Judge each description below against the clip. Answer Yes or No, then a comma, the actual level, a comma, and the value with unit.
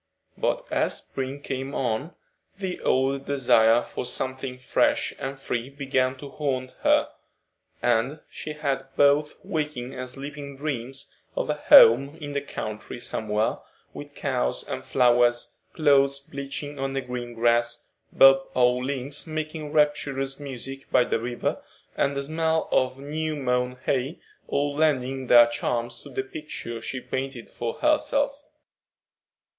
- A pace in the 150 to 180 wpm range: No, average, 140 wpm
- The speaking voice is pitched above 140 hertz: No, low, 135 Hz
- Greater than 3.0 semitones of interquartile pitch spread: No, narrow, 2.6 semitones